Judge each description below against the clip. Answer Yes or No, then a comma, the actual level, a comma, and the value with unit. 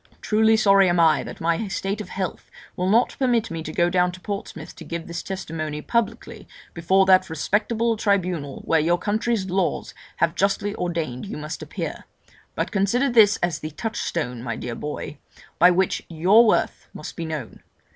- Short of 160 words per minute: No, average, 175 wpm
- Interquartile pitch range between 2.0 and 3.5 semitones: No, average, 3.9 semitones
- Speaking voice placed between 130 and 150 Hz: No, medium, 185 Hz